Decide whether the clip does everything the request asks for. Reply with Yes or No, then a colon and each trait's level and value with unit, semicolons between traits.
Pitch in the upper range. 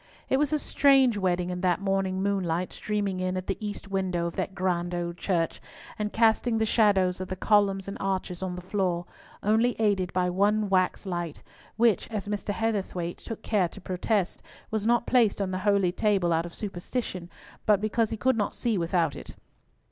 Yes: high, 195 Hz